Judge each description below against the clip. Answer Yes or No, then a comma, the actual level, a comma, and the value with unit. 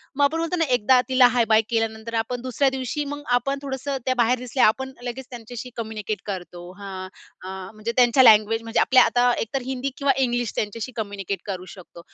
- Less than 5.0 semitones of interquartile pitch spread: Yes, average, 3.2 semitones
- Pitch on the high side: Yes, high, 240 Hz